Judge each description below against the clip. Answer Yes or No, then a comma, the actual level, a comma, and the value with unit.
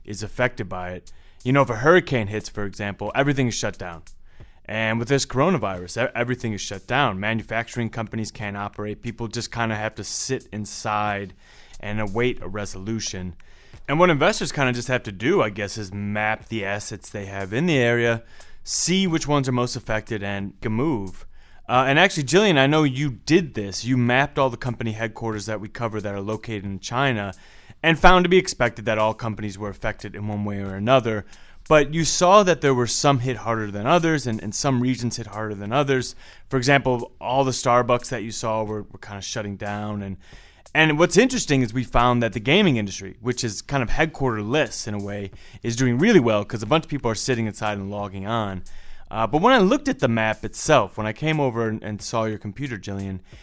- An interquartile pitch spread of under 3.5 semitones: No, average, 4.2 semitones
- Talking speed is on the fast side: Yes, fast, 215 wpm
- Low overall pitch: Yes, low, 115 Hz